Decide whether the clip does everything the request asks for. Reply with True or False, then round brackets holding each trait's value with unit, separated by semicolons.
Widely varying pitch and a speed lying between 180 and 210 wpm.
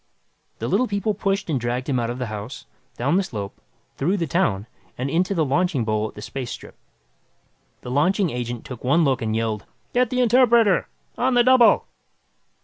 True (8.8 semitones; 190 wpm)